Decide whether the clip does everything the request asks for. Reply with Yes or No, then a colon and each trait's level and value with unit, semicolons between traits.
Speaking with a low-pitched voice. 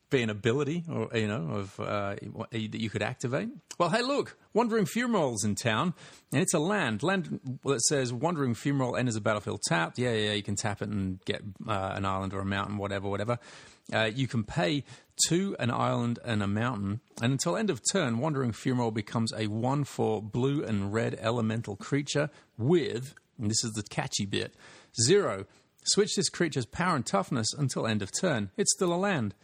Yes: low, 120 Hz